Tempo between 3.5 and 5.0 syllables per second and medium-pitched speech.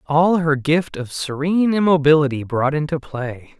Yes: 4.6 syllables/s; medium, 150 Hz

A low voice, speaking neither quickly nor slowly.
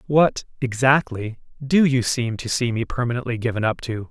Yes: low, 125 Hz; average, 145 wpm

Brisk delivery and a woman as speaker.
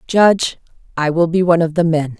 Yes: fast, 220 wpm; female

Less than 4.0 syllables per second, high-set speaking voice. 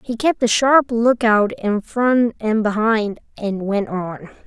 Yes: 3.7 syllables/s; high, 225 Hz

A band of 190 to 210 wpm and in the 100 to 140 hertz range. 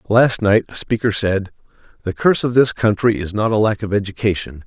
Yes: fast, 205 wpm; low, 105 Hz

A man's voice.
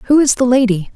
No: female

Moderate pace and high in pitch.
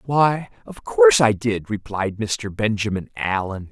No: average, 145 wpm; low, 120 Hz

